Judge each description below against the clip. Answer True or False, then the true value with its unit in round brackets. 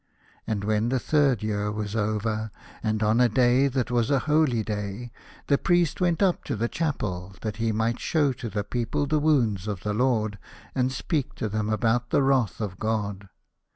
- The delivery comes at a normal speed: True (190 wpm)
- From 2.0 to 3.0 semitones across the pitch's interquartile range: False (4.0 semitones)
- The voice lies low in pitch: True (115 Hz)